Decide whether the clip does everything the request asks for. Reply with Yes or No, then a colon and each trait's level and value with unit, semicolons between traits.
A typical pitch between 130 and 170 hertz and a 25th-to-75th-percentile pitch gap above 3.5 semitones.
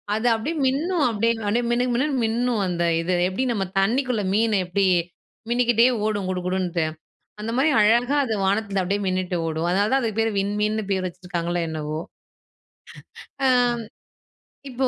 No: high, 210 Hz; average, 4.4 semitones